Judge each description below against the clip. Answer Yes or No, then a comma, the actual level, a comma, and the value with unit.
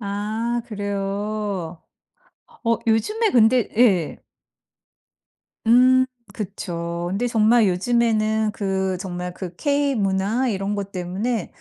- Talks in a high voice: Yes, high, 210 Hz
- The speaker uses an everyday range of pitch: Yes, average, 3.6 semitones